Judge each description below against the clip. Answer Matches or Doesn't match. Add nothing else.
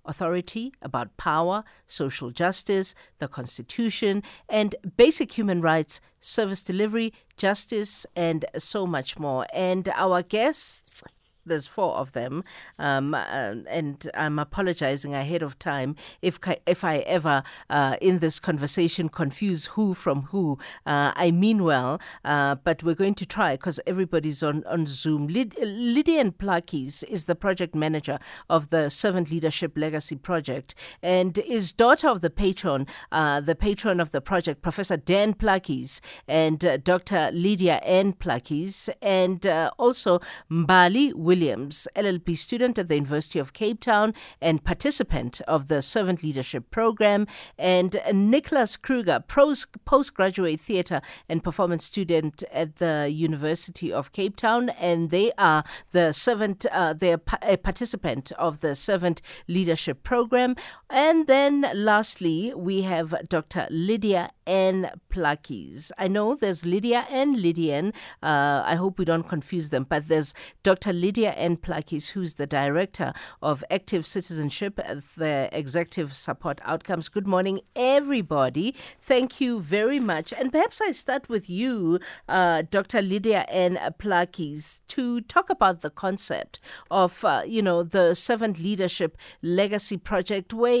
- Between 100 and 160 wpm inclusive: Matches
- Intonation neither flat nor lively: Matches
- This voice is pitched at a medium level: Matches